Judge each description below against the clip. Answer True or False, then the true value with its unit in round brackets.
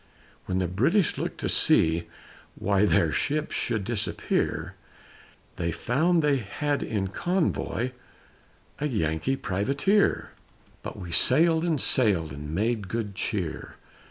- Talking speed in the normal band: False (125 wpm)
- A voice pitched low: True (110 Hz)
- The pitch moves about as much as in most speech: False (8.0 semitones)